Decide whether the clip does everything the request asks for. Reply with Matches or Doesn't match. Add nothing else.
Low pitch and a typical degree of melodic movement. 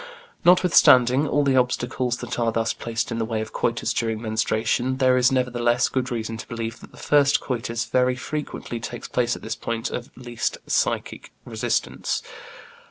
Doesn't match